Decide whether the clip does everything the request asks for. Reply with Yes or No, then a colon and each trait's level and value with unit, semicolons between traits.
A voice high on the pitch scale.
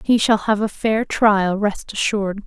Yes: high, 210 Hz